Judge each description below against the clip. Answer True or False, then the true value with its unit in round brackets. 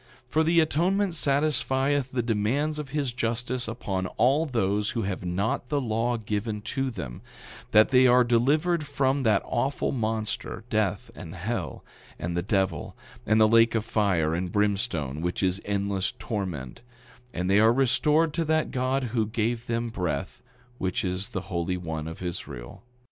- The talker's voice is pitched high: False (115 Hz)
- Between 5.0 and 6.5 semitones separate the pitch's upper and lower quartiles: True (5.6 semitones)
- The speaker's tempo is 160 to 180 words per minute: True (165 wpm)